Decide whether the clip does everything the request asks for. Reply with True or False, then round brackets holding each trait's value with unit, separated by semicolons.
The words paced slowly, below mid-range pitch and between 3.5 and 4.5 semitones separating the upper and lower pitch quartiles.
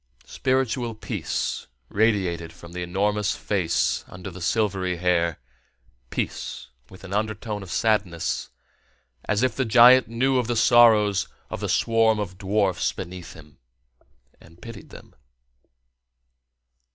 True (125 wpm; 105 Hz; 3.9 semitones)